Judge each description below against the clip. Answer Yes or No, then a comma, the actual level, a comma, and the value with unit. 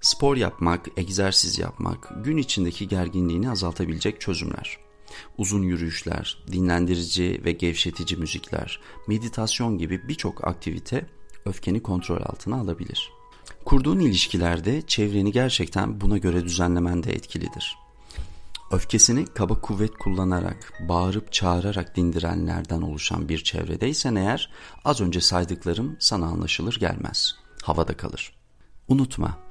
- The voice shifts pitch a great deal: No, average, 4.0 semitones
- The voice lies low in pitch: Yes, very low, 90 Hz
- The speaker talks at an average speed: Yes, average, 105 wpm